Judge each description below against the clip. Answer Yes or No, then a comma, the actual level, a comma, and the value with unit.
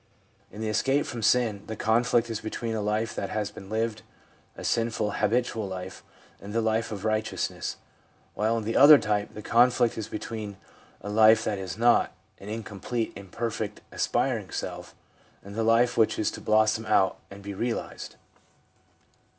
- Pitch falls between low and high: No, low, 110 Hz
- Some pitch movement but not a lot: No, narrow, 1.7 semitones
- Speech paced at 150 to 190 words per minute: Yes, average, 180 wpm